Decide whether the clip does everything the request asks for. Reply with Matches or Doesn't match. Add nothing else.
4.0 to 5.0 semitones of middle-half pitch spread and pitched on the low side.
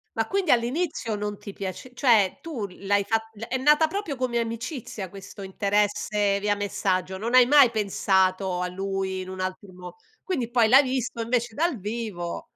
Doesn't match